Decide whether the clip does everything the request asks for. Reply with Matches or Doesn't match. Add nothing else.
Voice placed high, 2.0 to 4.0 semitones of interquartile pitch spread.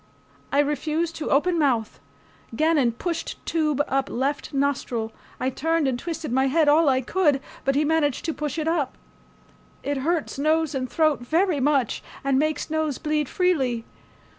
Matches